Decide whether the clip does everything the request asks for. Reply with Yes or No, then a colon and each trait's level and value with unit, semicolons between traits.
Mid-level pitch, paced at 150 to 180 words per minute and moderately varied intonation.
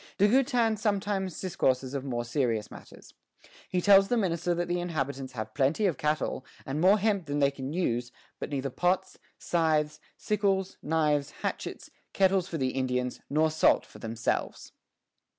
No: medium, 160 Hz; average, 160 wpm; wide, 6.1 semitones